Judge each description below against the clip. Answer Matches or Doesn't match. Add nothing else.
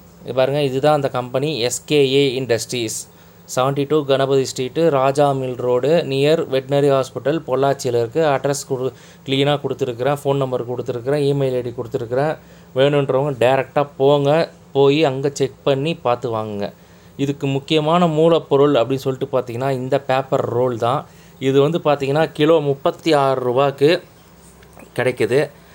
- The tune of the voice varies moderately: Doesn't match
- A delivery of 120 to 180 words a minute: Matches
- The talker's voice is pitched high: Doesn't match